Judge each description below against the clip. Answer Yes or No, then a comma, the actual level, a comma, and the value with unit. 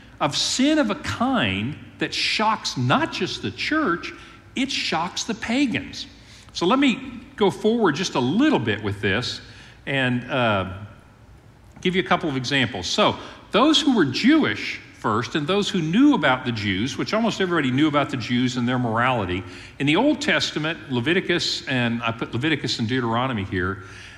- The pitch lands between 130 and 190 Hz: Yes, medium, 140 Hz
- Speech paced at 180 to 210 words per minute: No, average, 170 wpm